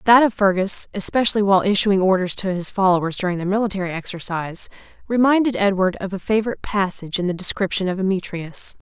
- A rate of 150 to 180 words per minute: Yes, average, 170 wpm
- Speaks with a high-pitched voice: Yes, high, 195 Hz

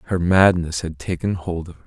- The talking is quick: Yes, fast, 225 wpm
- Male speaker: Yes, male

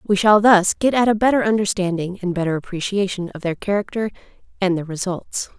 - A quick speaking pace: No, average, 185 wpm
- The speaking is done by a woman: Yes, female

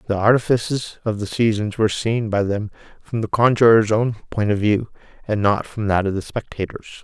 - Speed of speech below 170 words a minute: No, average, 195 wpm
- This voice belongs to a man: Yes, male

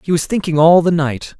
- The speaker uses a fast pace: Yes, fast, 260 wpm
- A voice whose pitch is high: No, medium, 165 Hz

